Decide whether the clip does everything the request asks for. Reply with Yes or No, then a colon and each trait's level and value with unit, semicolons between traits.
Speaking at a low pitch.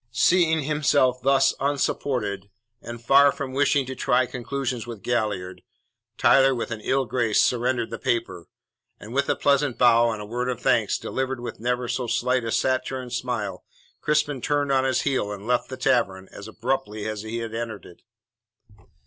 Yes: low, 125 Hz